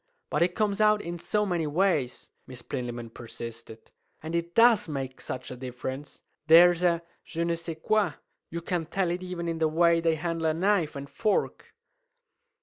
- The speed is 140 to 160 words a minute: No, average, 180 wpm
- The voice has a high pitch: No, medium, 165 Hz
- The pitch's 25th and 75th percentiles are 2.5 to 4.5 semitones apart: Yes, average, 4.1 semitones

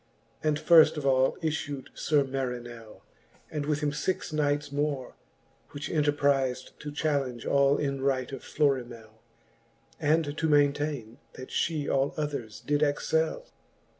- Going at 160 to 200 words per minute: No, slow, 135 wpm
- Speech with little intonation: Yes, narrow, 2.2 semitones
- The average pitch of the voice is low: No, medium, 145 Hz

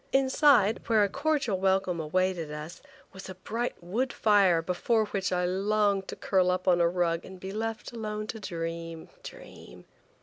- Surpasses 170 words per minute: No, average, 165 wpm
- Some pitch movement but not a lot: Yes, average, 3.5 semitones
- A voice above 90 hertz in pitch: Yes, high, 190 Hz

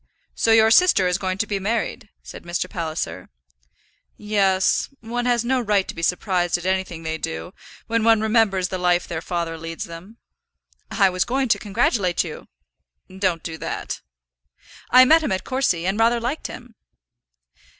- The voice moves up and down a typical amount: Yes, average, 4.5 semitones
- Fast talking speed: No, average, 170 wpm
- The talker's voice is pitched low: No, high, 195 Hz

